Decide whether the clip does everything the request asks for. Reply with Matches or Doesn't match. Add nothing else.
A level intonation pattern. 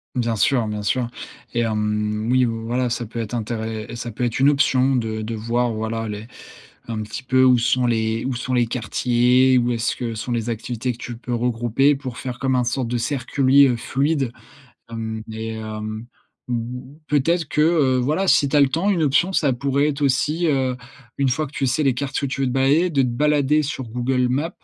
Doesn't match